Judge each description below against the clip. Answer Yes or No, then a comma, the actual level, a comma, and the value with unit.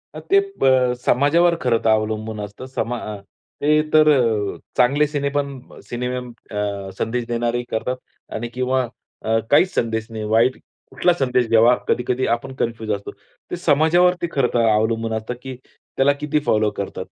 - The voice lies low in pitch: Yes, low, 125 Hz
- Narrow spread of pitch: No, average, 3.8 semitones